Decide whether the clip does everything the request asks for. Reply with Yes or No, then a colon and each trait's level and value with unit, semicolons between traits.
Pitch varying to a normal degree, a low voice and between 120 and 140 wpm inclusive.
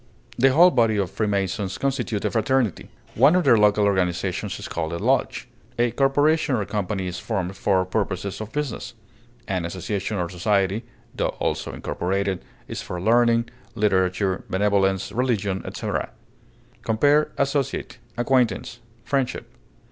Yes: average, 4.4 semitones; low, 105 Hz; slow, 135 wpm